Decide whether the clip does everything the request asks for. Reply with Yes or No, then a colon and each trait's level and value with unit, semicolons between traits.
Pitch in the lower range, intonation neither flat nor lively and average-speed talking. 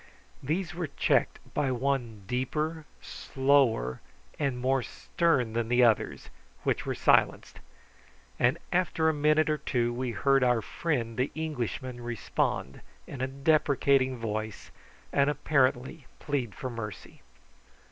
No: low, 130 Hz; average, 3.6 semitones; slow, 125 wpm